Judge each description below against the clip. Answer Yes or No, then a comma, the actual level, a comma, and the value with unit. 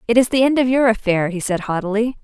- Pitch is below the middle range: No, high, 225 Hz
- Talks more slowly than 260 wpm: No, fast, 270 wpm